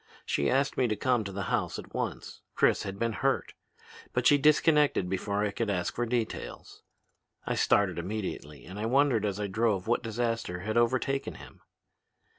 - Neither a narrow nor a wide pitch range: Yes, average, 3.7 semitones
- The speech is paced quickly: No, average, 180 wpm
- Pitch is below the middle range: Yes, low, 110 Hz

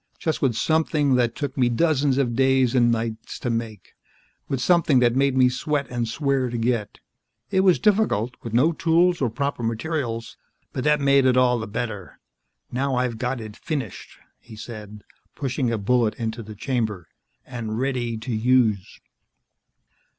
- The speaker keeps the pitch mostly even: No, average, 3.3 semitones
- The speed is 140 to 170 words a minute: Yes, average, 165 wpm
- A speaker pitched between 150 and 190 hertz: No, low, 125 Hz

